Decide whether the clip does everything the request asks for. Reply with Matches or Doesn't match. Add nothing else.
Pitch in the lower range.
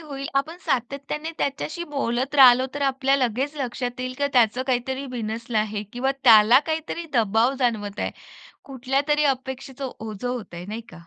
Doesn't match